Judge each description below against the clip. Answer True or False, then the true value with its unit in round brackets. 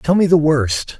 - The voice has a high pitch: False (155 Hz)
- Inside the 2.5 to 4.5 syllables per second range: True (4.2 syllables/s)